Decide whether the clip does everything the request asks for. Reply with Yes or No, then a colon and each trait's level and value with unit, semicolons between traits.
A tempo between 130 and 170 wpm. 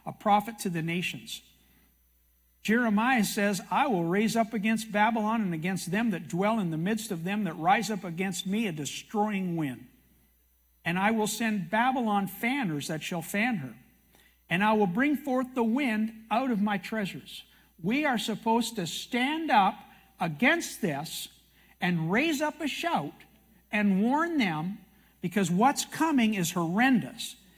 Yes: average, 160 wpm